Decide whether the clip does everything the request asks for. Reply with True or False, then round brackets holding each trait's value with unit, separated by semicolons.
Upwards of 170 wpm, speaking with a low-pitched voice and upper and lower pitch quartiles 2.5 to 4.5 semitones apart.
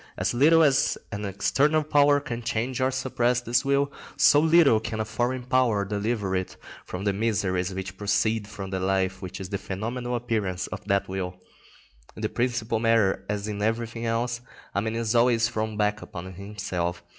True (180 wpm; 110 Hz; 3.8 semitones)